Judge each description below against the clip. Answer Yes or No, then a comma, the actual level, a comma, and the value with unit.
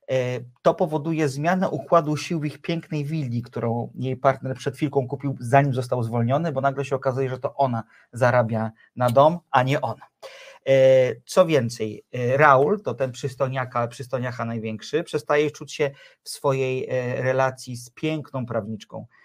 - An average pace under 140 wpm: No, average, 150 wpm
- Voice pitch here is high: No, low, 135 Hz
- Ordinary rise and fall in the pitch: Yes, average, 3.5 semitones